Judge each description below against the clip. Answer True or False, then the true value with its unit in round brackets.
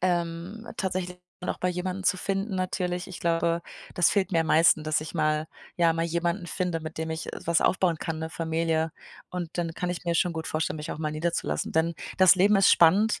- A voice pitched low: False (170 Hz)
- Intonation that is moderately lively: False (2.1 semitones)